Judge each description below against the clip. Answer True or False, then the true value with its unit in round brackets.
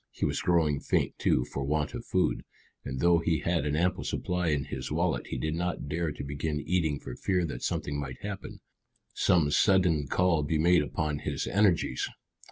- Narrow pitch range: False (3.3 semitones)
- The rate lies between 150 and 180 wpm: False (190 wpm)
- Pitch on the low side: True (80 Hz)